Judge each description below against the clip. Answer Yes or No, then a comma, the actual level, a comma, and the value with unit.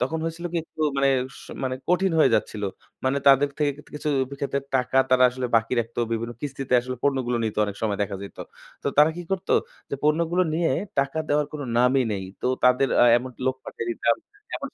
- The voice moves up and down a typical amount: Yes, average, 3.6 semitones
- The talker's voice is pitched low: Yes, low, 130 Hz